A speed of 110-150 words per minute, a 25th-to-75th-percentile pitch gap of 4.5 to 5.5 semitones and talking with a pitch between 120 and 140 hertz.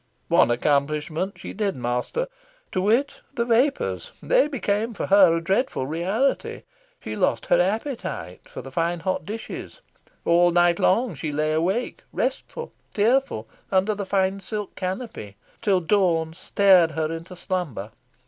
No: average, 145 wpm; average, 5.1 semitones; medium, 185 Hz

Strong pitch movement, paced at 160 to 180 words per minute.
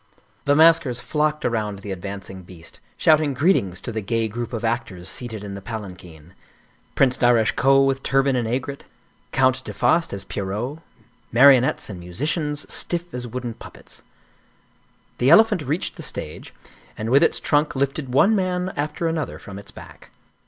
Yes: wide, 6.0 semitones; average, 165 wpm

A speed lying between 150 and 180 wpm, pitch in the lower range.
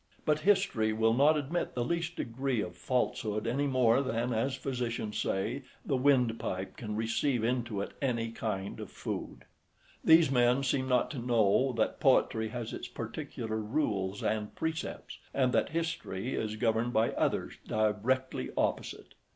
Yes: average, 160 wpm; low, 120 Hz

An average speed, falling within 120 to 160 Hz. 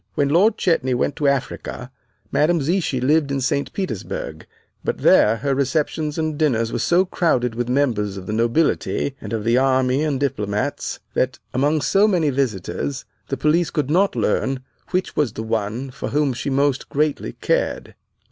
Yes: average, 170 wpm; medium, 140 Hz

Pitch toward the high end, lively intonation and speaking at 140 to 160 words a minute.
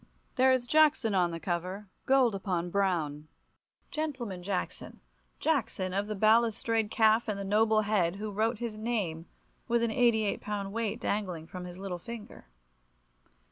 No: high, 210 Hz; average, 3.7 semitones; average, 150 wpm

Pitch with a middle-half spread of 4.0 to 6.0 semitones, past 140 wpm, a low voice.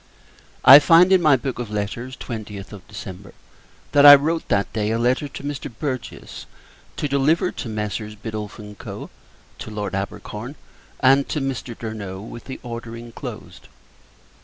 Yes: average, 4.7 semitones; average, 160 wpm; low, 115 Hz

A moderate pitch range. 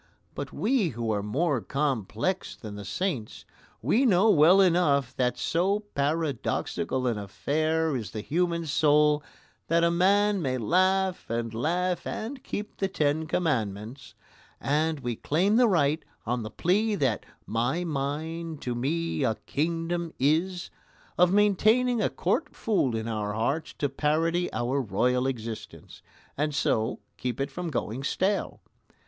No: wide, 6.1 semitones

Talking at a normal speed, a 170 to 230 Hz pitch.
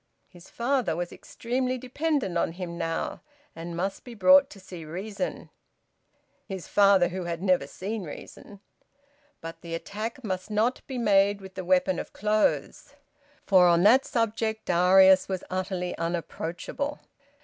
Yes: average, 145 wpm; high, 190 Hz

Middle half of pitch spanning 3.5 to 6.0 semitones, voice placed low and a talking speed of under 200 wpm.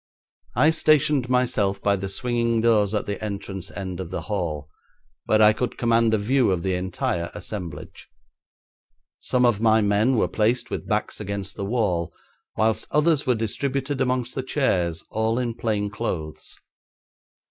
Yes: average, 4.2 semitones; low, 110 Hz; average, 160 wpm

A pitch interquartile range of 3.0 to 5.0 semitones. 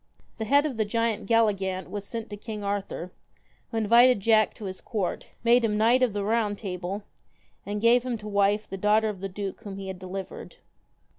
No: narrow, 2.6 semitones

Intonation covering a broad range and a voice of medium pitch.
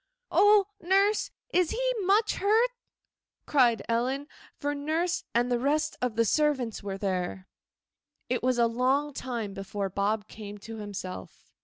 No: wide, 6.9 semitones; very high, 250 Hz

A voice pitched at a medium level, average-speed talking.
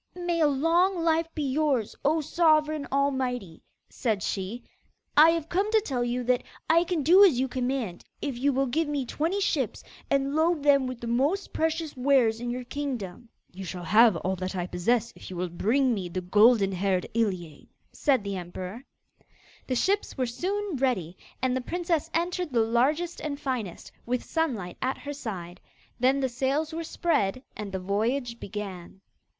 No: very high, 255 Hz; average, 180 wpm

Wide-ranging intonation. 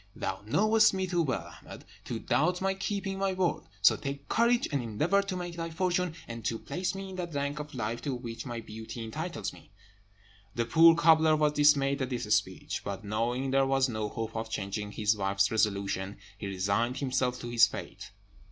Yes: wide, 7.3 semitones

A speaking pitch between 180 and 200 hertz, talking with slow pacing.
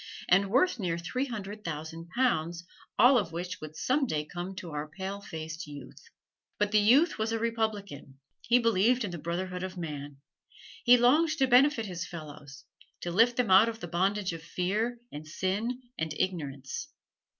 No: high, 190 Hz; average, 175 wpm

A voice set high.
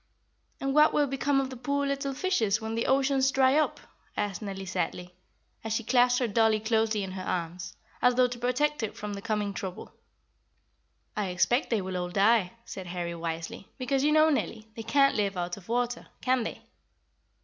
Yes: high, 225 Hz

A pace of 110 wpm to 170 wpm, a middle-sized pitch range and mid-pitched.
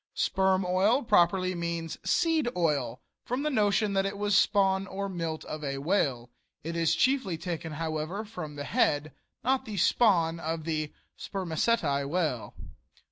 Yes: average, 150 wpm; average, 4.3 semitones; medium, 175 Hz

